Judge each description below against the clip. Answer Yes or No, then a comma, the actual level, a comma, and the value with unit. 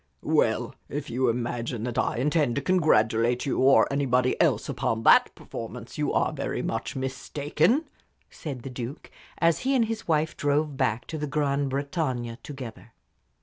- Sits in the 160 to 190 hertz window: No, low, 135 Hz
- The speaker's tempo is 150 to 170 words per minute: Yes, average, 160 wpm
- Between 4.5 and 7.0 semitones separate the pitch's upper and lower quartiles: No, average, 3.7 semitones